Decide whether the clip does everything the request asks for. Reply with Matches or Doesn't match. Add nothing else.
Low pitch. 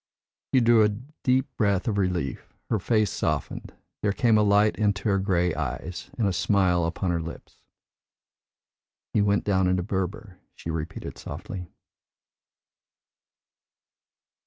Matches